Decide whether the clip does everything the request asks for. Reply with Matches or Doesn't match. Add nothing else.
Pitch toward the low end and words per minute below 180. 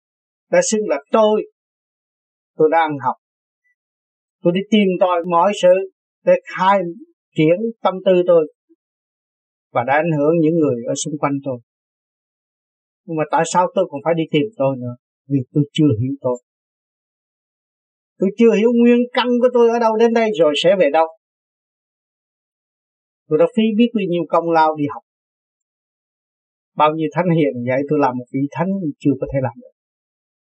Doesn't match